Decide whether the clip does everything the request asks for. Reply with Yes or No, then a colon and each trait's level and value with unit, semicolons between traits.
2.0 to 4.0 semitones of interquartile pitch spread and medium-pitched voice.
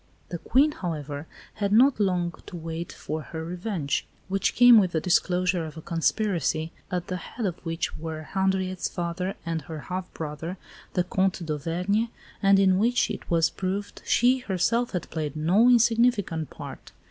Yes: average, 3.5 semitones; medium, 180 Hz